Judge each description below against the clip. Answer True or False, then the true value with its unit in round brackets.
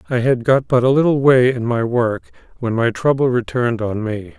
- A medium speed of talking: False (220 wpm)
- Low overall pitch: True (125 Hz)